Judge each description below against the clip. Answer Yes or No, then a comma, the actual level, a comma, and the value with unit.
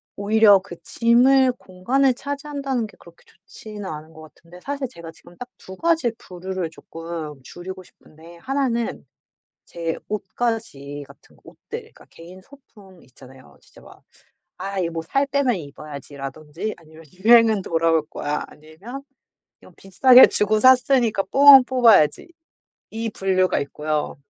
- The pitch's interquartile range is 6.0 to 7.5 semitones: Yes, wide, 6.9 semitones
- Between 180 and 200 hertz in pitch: Yes, high, 190 Hz